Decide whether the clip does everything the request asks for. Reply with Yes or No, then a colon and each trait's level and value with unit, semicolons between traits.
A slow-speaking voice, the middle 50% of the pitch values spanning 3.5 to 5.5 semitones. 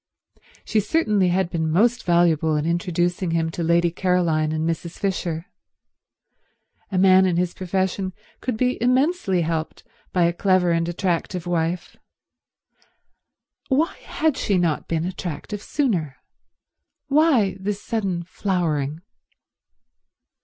No: slow, 120 wpm; average, 3.0 semitones